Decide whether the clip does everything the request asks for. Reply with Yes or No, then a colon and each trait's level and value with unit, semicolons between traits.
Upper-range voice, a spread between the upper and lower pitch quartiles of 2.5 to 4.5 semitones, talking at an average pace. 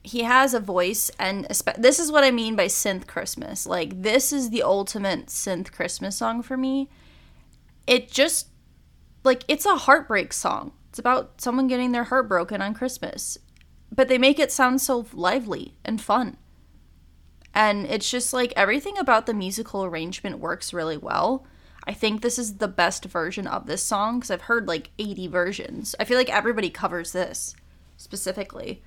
No: high, 220 Hz; wide, 5.4 semitones; average, 175 wpm